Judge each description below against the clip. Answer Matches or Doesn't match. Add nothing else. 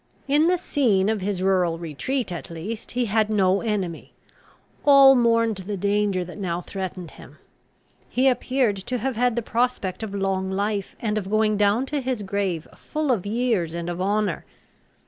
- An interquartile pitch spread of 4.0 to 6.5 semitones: Matches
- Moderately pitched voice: Doesn't match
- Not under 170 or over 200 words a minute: Matches